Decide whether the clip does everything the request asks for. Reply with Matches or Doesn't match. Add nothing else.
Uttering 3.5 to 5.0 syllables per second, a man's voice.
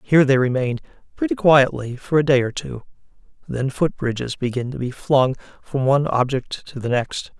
Doesn't match